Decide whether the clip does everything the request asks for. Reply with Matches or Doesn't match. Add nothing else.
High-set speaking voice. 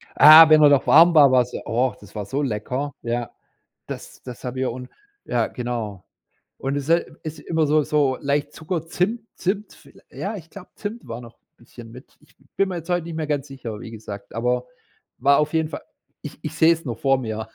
Doesn't match